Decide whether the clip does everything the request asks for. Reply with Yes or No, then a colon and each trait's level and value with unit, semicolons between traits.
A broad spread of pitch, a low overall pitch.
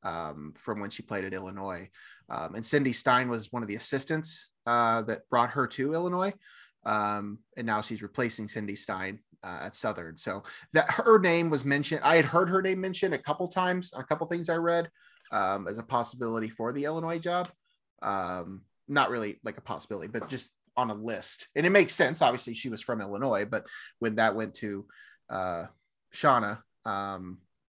Yes: wide, 7.9 semitones; low, 120 Hz